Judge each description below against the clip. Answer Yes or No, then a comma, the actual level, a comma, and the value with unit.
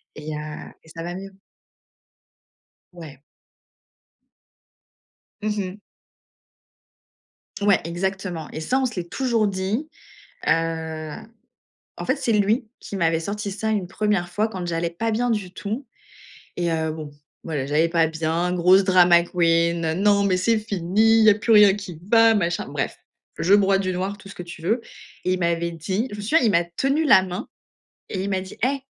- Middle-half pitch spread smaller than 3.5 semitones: No, average, 3.8 semitones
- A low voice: No, medium, 185 Hz